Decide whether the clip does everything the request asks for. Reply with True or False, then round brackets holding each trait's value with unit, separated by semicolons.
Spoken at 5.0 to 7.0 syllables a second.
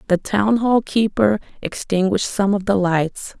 False (4.4 syllables/s)